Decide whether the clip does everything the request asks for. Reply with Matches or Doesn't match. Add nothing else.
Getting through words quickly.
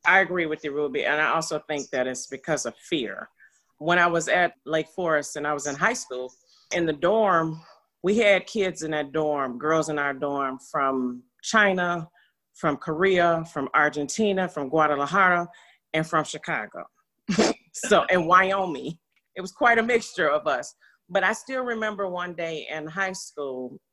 Doesn't match